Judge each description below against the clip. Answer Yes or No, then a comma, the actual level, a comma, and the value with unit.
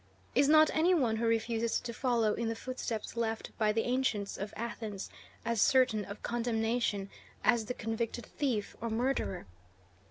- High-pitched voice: Yes, high, 230 Hz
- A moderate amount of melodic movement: No, narrow, 2.1 semitones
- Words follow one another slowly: No, average, 160 wpm